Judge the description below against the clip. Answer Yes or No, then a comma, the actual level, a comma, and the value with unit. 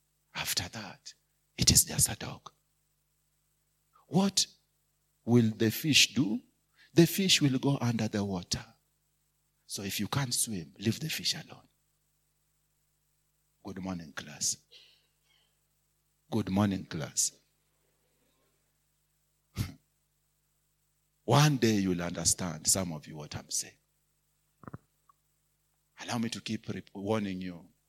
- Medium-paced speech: No, slow, 110 wpm